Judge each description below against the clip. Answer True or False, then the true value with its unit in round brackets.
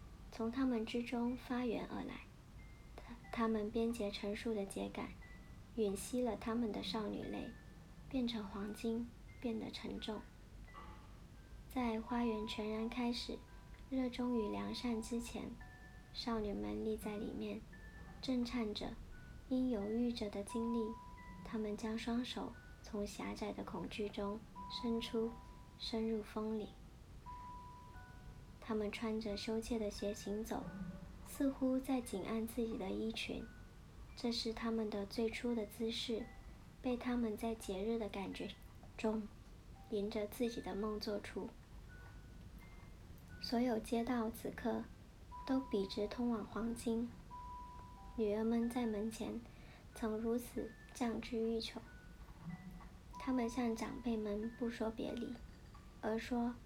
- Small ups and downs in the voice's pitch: True (2.2 semitones)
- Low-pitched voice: False (225 Hz)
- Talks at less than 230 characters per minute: True (180 characters per minute)